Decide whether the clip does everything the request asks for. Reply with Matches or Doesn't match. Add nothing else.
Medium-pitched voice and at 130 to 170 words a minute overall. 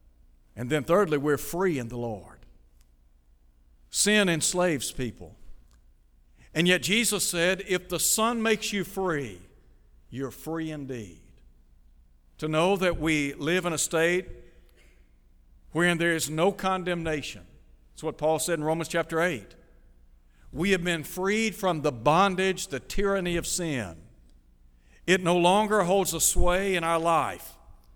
Matches